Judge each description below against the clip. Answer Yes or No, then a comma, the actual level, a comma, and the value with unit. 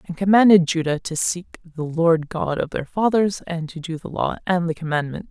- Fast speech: Yes, fast, 215 wpm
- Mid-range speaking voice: Yes, medium, 170 Hz